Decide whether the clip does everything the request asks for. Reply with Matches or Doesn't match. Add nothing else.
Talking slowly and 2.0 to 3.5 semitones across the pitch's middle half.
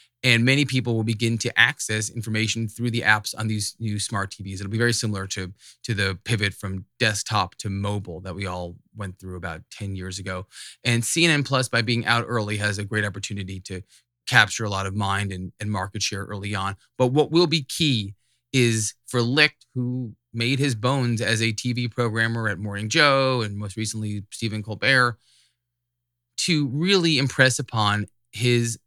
Doesn't match